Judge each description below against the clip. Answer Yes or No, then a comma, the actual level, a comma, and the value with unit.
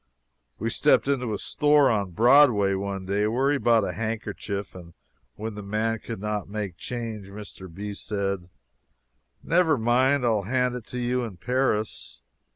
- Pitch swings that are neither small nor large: Yes, average, 3.9 semitones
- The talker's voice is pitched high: No, low, 110 Hz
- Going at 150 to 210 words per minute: Yes, average, 160 wpm